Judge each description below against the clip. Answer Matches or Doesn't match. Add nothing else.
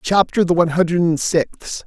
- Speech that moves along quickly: Doesn't match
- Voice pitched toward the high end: Doesn't match